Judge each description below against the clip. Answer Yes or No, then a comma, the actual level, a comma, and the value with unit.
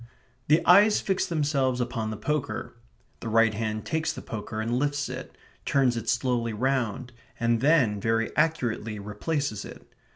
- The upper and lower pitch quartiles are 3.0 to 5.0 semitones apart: Yes, average, 4.6 semitones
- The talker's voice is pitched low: Yes, low, 120 Hz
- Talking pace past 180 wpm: No, average, 155 wpm